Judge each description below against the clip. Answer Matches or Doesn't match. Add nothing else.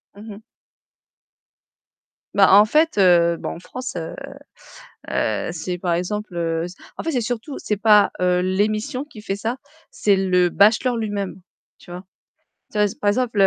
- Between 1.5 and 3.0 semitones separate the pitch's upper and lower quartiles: Doesn't match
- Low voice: Doesn't match